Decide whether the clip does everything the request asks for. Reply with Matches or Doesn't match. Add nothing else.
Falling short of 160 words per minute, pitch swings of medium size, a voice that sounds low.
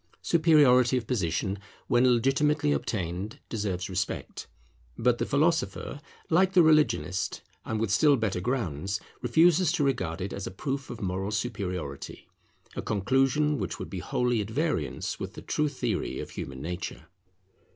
Doesn't match